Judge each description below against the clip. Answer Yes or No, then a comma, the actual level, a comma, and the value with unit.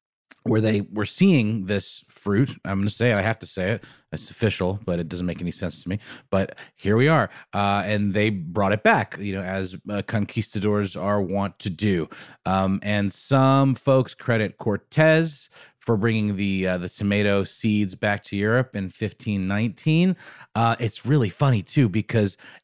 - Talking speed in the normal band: Yes, average, 185 wpm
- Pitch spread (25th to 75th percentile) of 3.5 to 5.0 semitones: No, average, 2.7 semitones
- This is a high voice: No, low, 105 Hz